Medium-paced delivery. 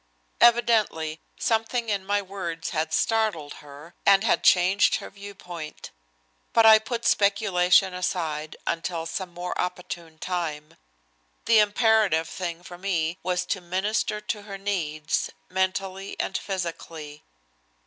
No: slow, 125 wpm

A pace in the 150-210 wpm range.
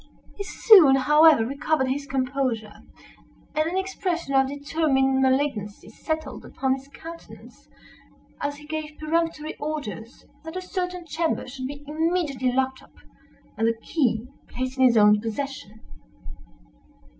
No: slow, 135 wpm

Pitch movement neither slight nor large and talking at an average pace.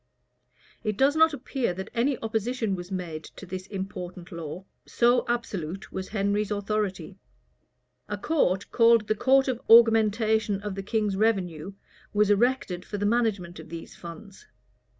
Yes: average, 3.5 semitones; average, 150 wpm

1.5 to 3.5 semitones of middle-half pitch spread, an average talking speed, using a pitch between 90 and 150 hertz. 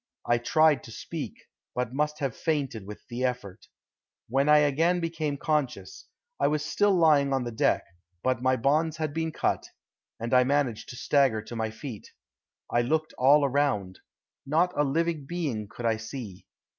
No: average, 4.3 semitones; average, 170 wpm; medium, 140 Hz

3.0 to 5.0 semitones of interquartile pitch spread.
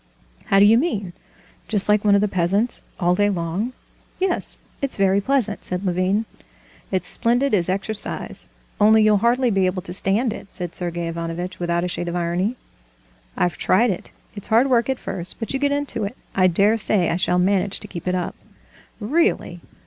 Yes: average, 3.9 semitones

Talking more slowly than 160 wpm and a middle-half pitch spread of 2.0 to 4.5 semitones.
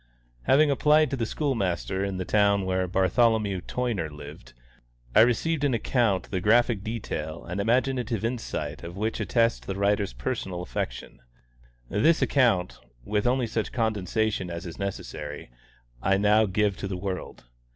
Yes: average, 150 wpm; average, 4.2 semitones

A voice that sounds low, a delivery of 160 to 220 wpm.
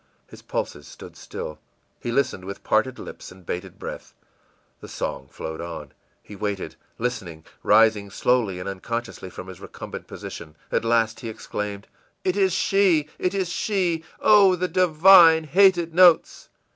No: low, 120 Hz; average, 145 wpm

